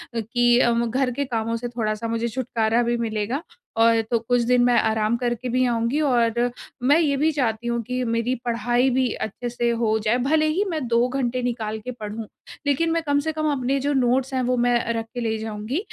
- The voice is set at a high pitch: Yes, high, 240 Hz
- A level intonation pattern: Yes, narrow, 2.2 semitones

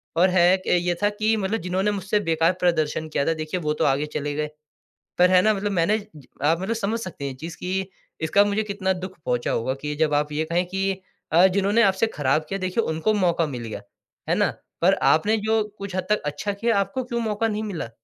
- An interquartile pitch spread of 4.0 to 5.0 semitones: Yes, average, 4.5 semitones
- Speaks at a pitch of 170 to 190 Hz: Yes, medium, 185 Hz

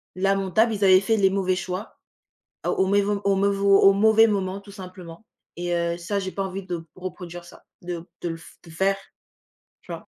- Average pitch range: No, narrow, 2.1 semitones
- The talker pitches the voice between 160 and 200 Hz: Yes, high, 190 Hz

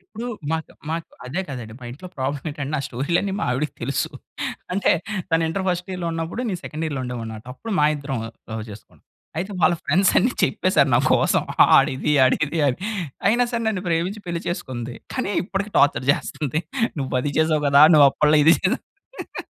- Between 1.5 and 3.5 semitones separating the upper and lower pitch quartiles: No, average, 5.1 semitones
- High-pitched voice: No, medium, 155 Hz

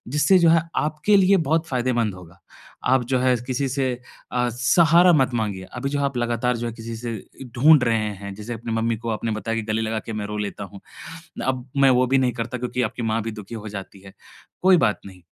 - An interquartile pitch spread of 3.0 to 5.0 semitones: Yes, average, 3.6 semitones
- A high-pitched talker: No, low, 120 Hz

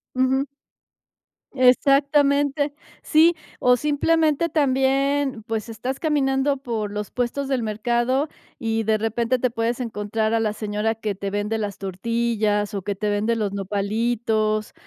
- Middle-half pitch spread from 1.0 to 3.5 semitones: No, average, 4.1 semitones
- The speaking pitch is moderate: No, high, 235 Hz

